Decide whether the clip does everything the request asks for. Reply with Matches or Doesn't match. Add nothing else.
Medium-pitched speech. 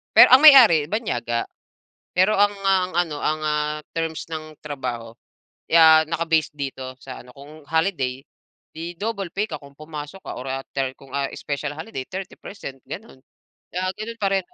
Matches